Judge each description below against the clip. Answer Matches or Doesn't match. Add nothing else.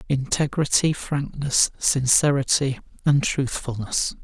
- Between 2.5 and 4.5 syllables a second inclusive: Matches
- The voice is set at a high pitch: Doesn't match